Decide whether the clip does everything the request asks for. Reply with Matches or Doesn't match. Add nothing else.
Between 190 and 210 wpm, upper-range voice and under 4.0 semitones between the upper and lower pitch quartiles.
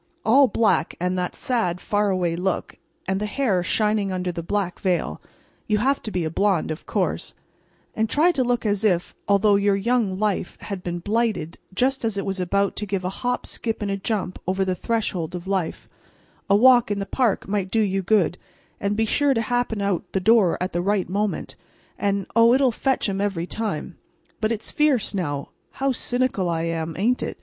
Matches